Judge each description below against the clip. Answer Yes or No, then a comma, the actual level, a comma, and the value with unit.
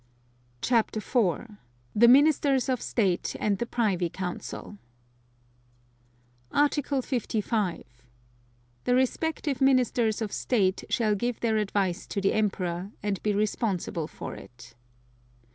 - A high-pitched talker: Yes, high, 215 Hz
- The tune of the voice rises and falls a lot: No, average, 4.2 semitones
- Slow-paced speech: Yes, slow, 110 wpm